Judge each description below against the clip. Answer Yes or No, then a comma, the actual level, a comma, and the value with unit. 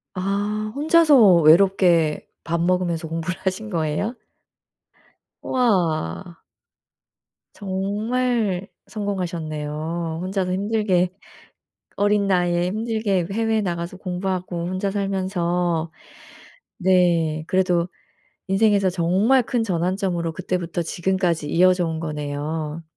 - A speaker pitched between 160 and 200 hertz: Yes, medium, 185 Hz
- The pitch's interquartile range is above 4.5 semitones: No, average, 3.0 semitones